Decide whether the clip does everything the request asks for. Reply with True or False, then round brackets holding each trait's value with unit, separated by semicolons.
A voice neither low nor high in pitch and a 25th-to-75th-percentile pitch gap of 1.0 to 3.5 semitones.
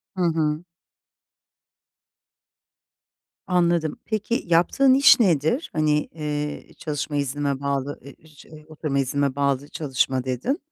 True (150 Hz; 3.2 semitones)